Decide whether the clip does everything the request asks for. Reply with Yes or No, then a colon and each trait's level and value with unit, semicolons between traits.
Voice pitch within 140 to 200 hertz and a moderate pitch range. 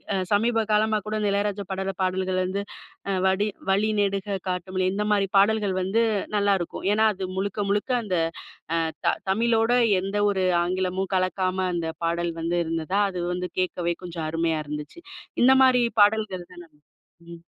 No: high, 190 Hz; narrow, 2.3 semitones